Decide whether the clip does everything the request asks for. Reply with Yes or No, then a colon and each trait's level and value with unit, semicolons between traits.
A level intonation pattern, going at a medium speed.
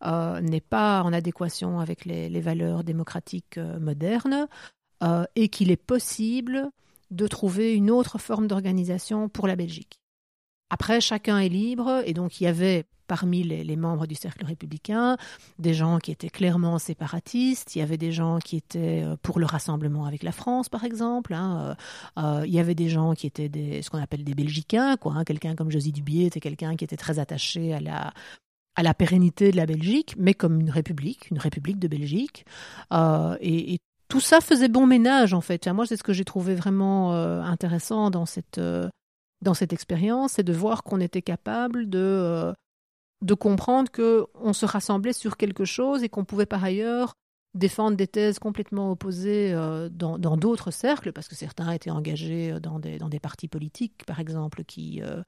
No: average, 4.6 semitones; average, 195 wpm